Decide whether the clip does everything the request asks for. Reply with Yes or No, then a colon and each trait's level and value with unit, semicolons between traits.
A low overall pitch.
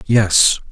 Yes: low, 105 Hz